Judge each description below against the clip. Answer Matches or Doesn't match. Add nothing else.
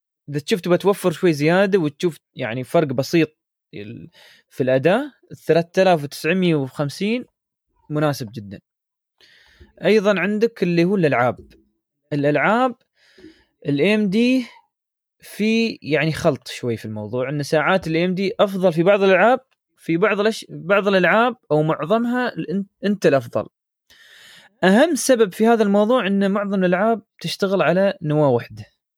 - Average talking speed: Matches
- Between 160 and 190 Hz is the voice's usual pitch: Matches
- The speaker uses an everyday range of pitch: Doesn't match